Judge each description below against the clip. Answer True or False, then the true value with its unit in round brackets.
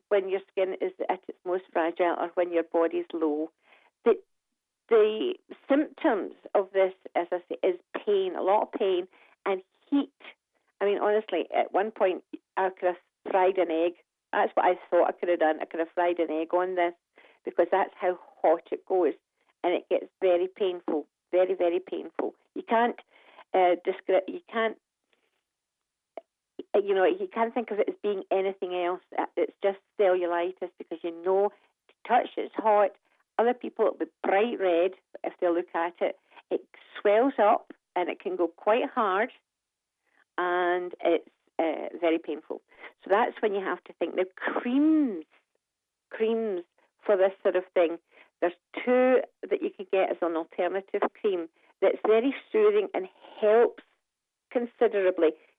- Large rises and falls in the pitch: True (7.7 semitones)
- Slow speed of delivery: False (165 wpm)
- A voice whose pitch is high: True (195 Hz)